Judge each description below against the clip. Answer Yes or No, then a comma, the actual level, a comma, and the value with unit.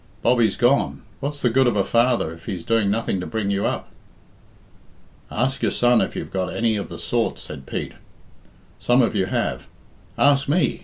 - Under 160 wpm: No, average, 190 wpm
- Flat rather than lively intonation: No, average, 4.2 semitones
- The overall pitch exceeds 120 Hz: No, low, 115 Hz